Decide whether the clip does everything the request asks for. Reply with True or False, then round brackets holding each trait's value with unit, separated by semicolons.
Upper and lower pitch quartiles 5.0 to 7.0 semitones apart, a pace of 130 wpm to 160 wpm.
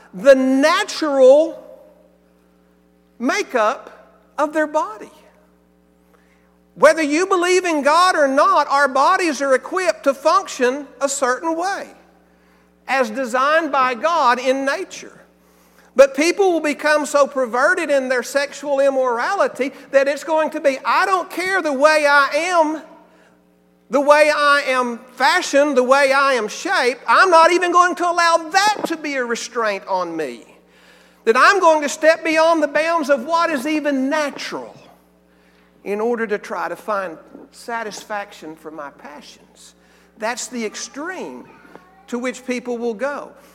True (5.3 semitones; 145 wpm)